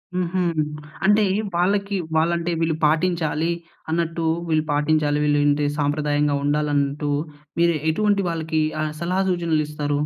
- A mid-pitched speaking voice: Yes, medium, 160 Hz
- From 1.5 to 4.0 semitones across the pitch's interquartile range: Yes, narrow, 2.6 semitones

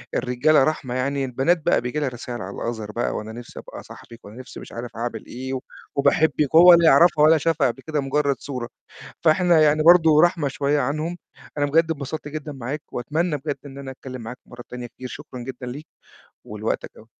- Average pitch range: Yes, average, 3.9 semitones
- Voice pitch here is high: No, medium, 140 Hz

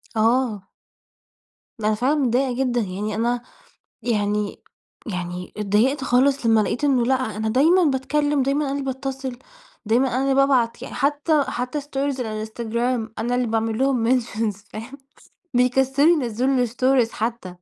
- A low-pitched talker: No, high, 245 Hz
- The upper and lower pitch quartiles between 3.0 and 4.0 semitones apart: Yes, average, 3.4 semitones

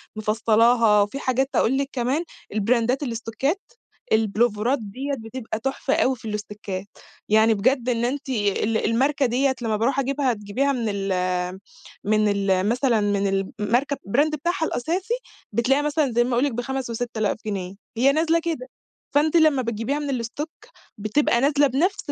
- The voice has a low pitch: No, high, 245 Hz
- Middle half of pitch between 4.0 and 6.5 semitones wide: Yes, average, 4.3 semitones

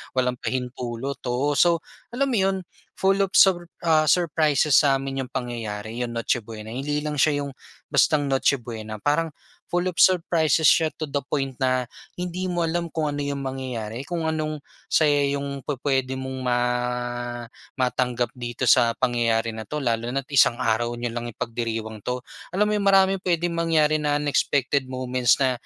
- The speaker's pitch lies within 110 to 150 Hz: Yes, low, 135 Hz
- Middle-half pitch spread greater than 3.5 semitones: Yes, average, 4.3 semitones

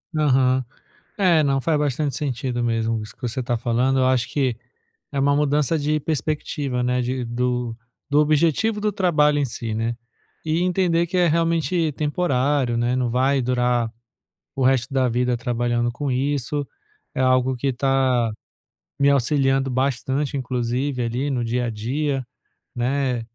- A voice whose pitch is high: No, low, 130 Hz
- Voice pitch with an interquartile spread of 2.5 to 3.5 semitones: Yes, average, 3.1 semitones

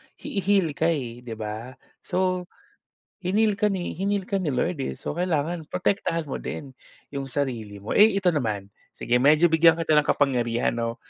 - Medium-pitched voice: Yes, medium, 155 Hz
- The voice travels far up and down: Yes, wide, 6.7 semitones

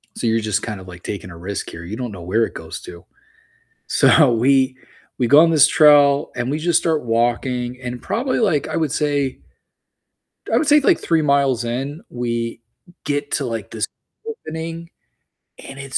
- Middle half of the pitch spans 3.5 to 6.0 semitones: Yes, average, 4.7 semitones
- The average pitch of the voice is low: Yes, low, 130 Hz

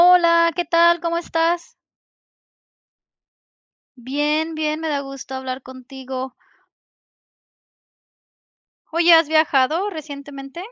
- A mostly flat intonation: No, average, 3.6 semitones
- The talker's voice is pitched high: Yes, very high, 310 Hz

